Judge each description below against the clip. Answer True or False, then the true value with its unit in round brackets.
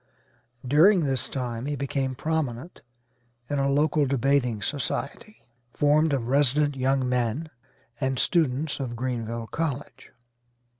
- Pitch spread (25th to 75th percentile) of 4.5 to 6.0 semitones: False (2.9 semitones)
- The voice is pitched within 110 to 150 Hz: True (135 Hz)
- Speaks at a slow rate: True (115 wpm)